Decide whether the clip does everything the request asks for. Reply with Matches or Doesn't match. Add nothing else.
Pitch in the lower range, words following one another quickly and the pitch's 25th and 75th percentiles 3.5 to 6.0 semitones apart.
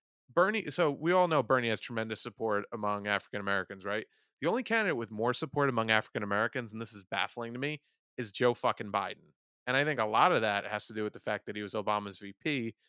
Matches